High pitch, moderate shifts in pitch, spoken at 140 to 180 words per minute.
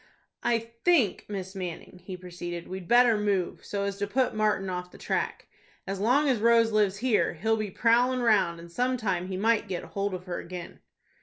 No: high, 205 Hz; average, 4.0 semitones; average, 200 wpm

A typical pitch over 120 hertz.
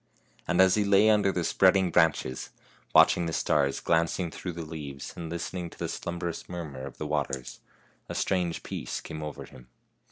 No: very low, 85 Hz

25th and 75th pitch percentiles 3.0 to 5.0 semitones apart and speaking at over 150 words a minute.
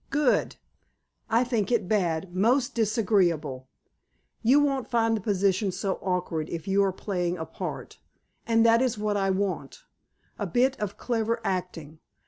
No: average, 4.2 semitones; average, 145 wpm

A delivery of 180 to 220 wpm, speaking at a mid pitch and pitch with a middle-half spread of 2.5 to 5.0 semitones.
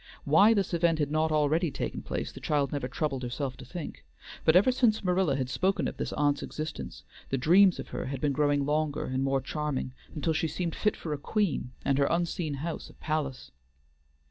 Yes: fast, 205 wpm; medium, 150 Hz; average, 3.6 semitones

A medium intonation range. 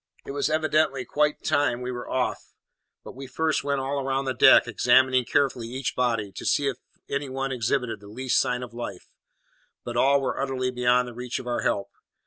No: narrow, 2.0 semitones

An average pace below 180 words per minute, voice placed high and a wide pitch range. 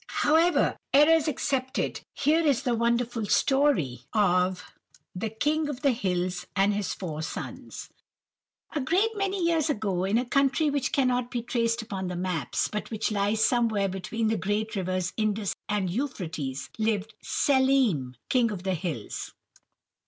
Yes: average, 150 wpm; high, 220 Hz; wide, 6.3 semitones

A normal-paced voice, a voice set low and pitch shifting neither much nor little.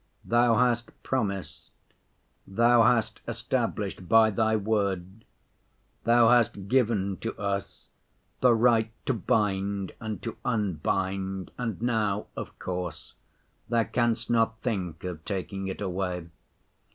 No: slow, 115 wpm; low, 105 Hz; average, 3.3 semitones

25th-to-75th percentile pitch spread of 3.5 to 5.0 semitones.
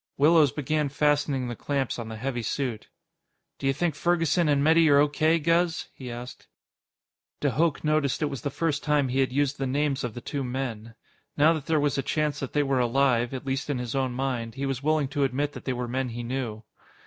No: average, 2.7 semitones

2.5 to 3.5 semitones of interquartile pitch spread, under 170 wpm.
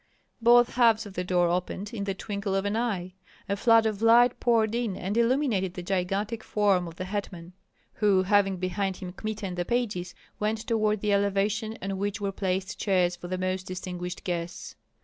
No: average, 2.9 semitones; average, 190 wpm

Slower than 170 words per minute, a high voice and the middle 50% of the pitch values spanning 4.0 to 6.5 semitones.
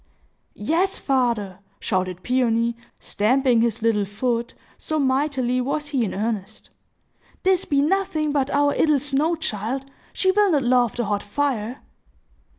Yes: average, 140 wpm; very high, 255 Hz; average, 4.4 semitones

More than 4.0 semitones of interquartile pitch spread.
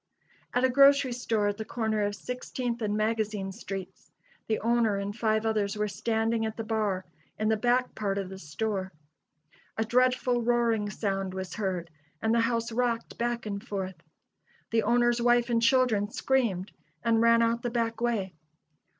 No: average, 2.7 semitones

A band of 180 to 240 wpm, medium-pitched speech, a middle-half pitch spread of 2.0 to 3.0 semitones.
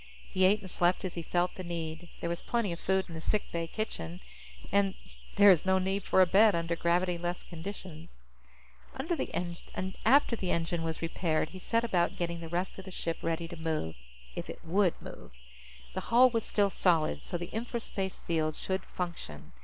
Yes: average, 195 wpm; medium, 175 Hz; narrow, 2.6 semitones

